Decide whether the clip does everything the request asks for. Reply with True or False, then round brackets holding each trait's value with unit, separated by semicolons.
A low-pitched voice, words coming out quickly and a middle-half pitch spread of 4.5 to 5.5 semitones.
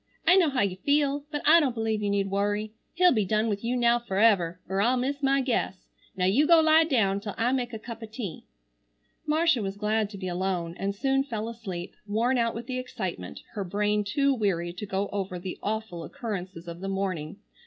False (215 Hz; 215 wpm; 4.8 semitones)